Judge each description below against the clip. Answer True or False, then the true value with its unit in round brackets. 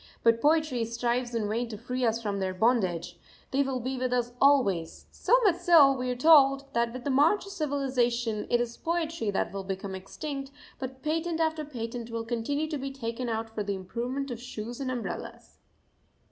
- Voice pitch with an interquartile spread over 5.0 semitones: False (3.6 semitones)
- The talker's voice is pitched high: True (245 Hz)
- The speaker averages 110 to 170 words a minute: False (195 wpm)